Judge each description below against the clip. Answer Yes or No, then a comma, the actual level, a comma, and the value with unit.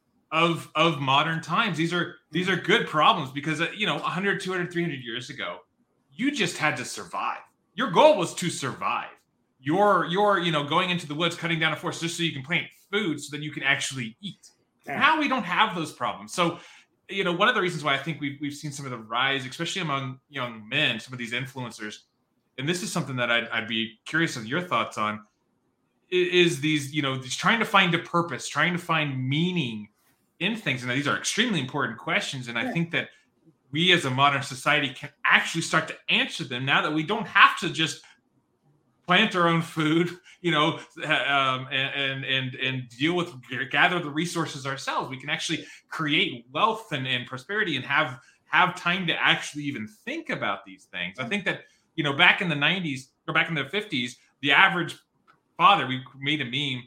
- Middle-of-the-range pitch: Yes, medium, 155 Hz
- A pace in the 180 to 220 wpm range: Yes, fast, 205 wpm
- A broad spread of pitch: No, average, 4.7 semitones